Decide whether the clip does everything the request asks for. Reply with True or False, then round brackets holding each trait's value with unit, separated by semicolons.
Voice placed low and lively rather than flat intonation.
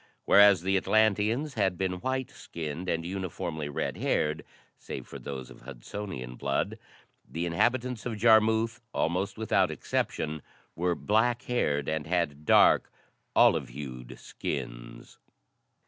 True (90 Hz; 6.4 semitones)